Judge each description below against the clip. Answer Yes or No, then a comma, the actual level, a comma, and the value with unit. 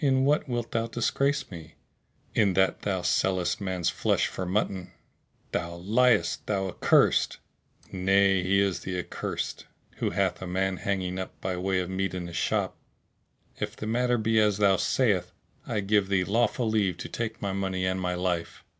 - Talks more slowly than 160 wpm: No, average, 175 wpm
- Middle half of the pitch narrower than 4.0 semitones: Yes, average, 2.7 semitones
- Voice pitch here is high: No, very low, 95 Hz